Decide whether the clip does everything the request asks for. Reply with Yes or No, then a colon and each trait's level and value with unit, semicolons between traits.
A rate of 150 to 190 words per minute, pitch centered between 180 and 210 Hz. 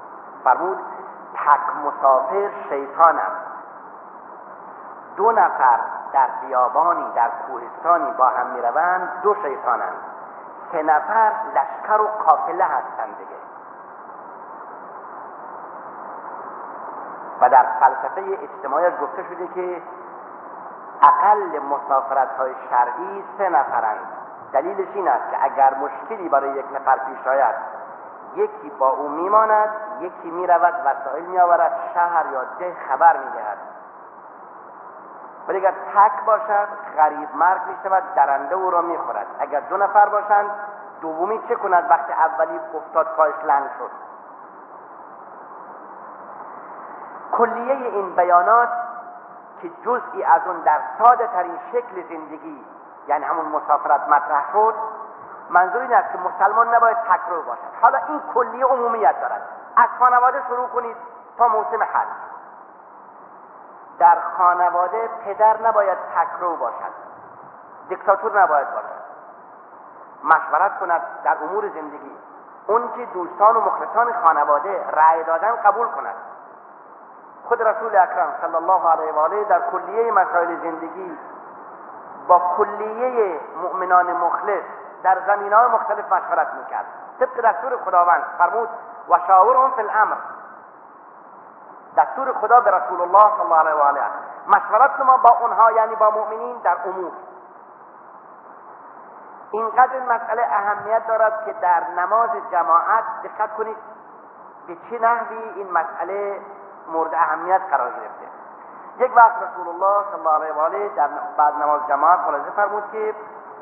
No: average, 125 wpm; high, 190 Hz